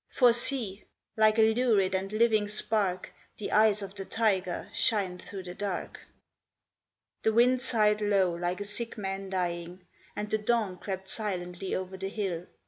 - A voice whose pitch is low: No, high, 200 Hz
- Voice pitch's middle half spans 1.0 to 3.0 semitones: Yes, narrow, 2.6 semitones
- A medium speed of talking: Yes, average, 160 wpm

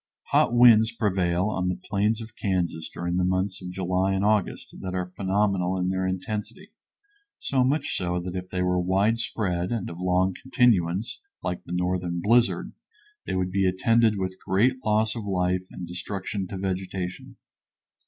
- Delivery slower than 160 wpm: No, average, 165 wpm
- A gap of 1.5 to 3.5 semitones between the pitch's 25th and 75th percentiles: Yes, average, 2.7 semitones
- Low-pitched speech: Yes, very low, 95 Hz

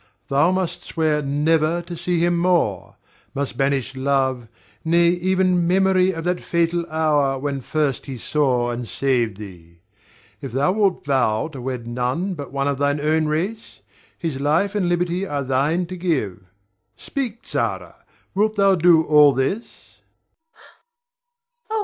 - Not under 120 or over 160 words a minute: Yes, average, 150 wpm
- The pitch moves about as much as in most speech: Yes, average, 4.6 semitones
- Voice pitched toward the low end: No, medium, 155 Hz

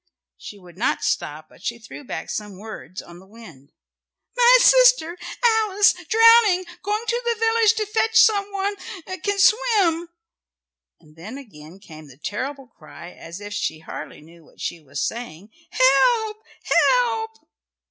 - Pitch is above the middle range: Yes, very high, 280 Hz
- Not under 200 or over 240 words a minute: No, average, 150 wpm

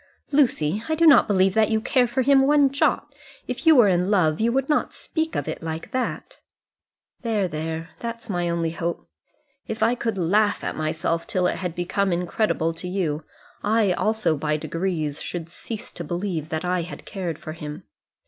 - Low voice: No, medium, 185 Hz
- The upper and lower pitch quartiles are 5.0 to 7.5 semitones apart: Yes, wide, 5.5 semitones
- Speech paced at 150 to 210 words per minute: Yes, average, 190 wpm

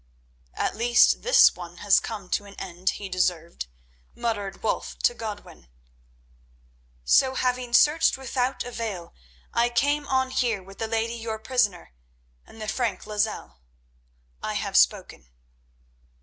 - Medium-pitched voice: No, high, 220 Hz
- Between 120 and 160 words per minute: Yes, slow, 135 wpm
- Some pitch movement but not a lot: Yes, average, 4.2 semitones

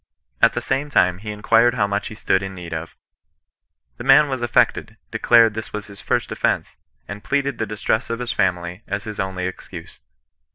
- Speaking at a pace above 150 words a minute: Yes, average, 200 wpm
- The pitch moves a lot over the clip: No, average, 3.6 semitones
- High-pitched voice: No, low, 105 Hz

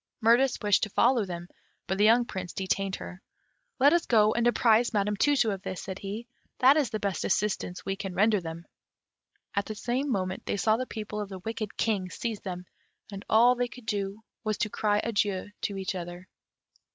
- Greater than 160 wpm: Yes, fast, 205 wpm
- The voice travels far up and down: No, average, 3.2 semitones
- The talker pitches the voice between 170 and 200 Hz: No, high, 210 Hz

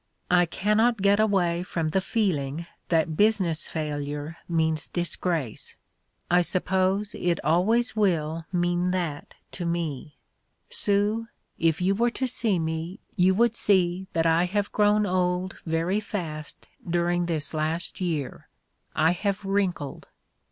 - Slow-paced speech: Yes, slow, 130 wpm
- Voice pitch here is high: No, medium, 175 Hz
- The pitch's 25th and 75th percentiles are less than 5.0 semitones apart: Yes, average, 3.6 semitones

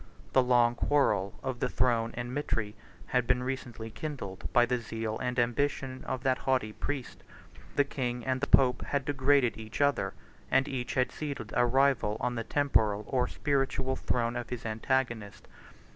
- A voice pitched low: Yes, low, 125 Hz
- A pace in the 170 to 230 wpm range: Yes, average, 175 wpm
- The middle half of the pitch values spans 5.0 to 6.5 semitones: No, narrow, 2.4 semitones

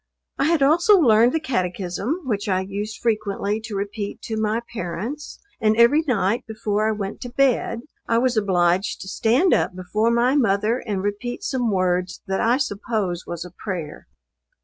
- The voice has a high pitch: Yes, high, 215 Hz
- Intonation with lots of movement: No, average, 3.8 semitones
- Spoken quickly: No, average, 170 wpm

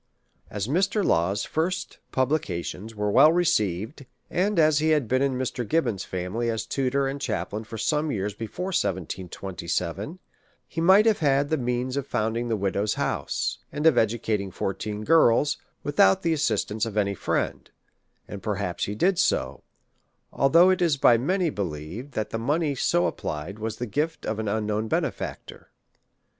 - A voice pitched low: Yes, low, 115 Hz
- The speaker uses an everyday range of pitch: No, wide, 6.8 semitones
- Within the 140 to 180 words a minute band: Yes, average, 160 wpm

